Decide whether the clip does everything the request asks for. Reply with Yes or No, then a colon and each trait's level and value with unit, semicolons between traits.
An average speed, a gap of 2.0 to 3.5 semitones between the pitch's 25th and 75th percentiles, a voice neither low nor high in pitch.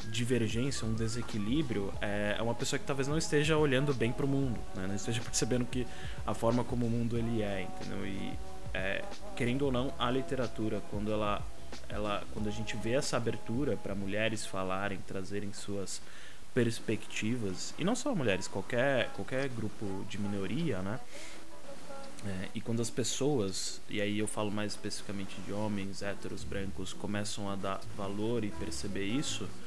No: average, 165 wpm; average, 3.2 semitones; low, 105 Hz